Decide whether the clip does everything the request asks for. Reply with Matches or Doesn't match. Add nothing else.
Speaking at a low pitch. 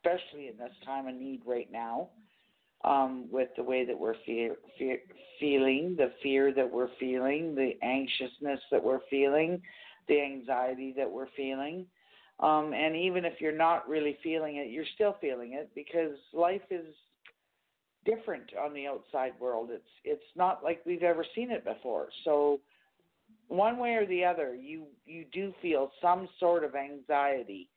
Doesn't match